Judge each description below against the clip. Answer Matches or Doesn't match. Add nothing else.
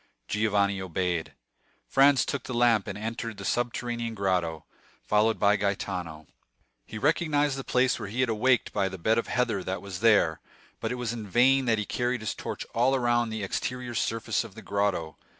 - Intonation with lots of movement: Doesn't match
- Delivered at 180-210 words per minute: Matches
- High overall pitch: Doesn't match